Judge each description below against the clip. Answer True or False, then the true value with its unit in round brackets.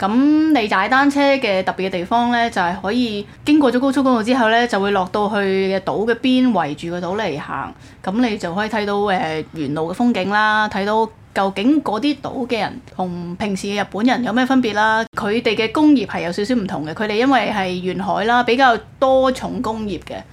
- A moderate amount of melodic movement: True (4.4 semitones)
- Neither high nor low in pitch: False (215 Hz)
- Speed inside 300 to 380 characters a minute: True (310 characters per minute)